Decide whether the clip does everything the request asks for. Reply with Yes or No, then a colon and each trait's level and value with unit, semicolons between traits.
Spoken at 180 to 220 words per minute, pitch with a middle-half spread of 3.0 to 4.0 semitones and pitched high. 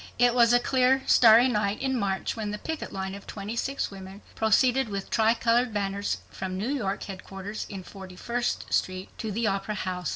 Yes: average, 190 wpm; average, 3.6 semitones; high, 210 Hz